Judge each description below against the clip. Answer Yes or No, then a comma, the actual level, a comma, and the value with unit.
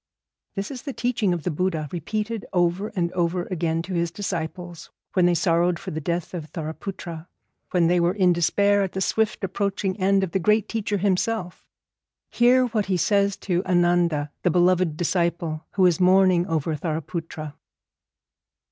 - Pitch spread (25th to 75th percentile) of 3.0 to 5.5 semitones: No, narrow, 2.6 semitones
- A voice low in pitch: No, medium, 180 Hz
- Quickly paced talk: No, average, 165 wpm